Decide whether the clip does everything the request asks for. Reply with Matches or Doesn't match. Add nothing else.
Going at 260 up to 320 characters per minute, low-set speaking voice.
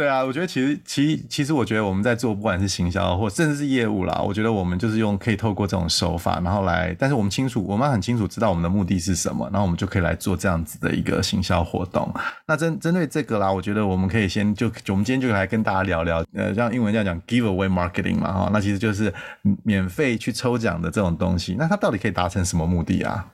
Doesn't match